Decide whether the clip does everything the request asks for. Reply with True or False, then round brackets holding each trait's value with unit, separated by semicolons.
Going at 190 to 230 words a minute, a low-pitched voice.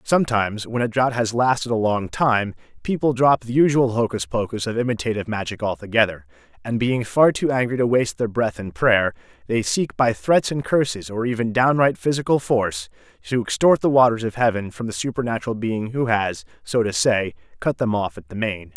True (200 wpm; 115 Hz)